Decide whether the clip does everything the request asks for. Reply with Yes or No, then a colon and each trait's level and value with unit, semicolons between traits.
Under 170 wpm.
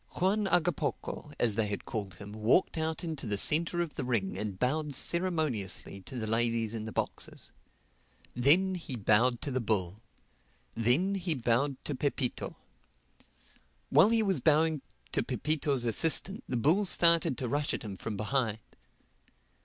Yes: average, 155 wpm